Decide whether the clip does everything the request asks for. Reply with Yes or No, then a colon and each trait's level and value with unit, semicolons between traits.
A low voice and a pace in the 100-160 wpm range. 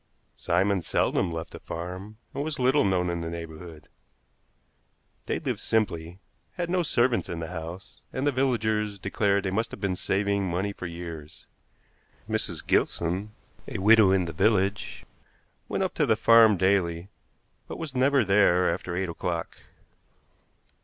Yes: very low, 95 Hz; average, 155 wpm